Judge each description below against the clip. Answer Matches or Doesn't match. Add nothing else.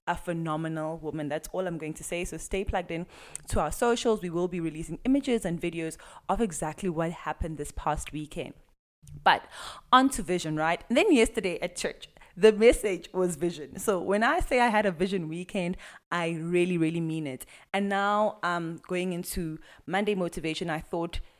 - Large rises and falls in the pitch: Doesn't match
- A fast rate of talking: Doesn't match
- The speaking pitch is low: Doesn't match